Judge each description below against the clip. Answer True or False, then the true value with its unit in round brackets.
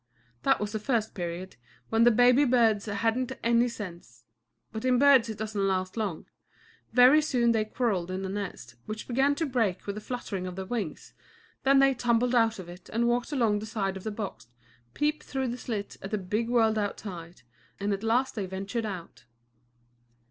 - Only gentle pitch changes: False (3.9 semitones)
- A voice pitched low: False (220 Hz)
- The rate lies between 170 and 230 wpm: True (190 wpm)